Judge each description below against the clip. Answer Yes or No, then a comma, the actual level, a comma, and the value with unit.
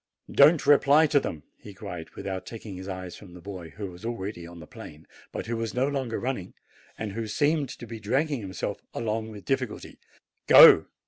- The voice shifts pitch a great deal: Yes, wide, 5.8 semitones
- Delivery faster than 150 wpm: Yes, average, 195 wpm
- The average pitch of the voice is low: Yes, low, 110 Hz